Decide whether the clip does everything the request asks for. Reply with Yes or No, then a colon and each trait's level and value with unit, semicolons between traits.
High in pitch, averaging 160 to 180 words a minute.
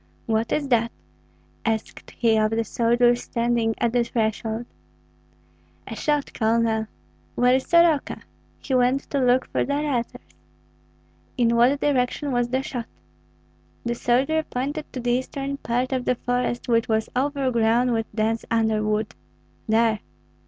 No: high, 240 Hz; average, 140 wpm